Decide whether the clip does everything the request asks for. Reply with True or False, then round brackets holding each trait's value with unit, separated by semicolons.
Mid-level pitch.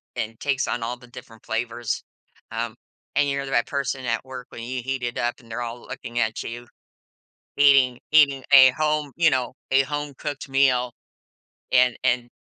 False (125 Hz)